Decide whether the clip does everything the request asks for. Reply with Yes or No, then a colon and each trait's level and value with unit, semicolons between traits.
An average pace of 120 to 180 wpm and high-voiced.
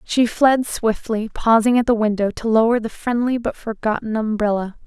Yes: average, 175 wpm; high, 225 Hz